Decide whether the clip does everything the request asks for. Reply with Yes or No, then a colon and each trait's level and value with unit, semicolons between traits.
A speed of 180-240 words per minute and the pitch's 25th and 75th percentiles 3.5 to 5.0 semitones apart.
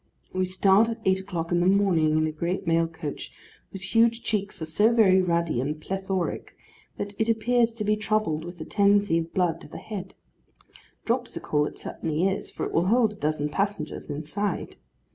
Yes: average, 190 wpm; average, 4.2 semitones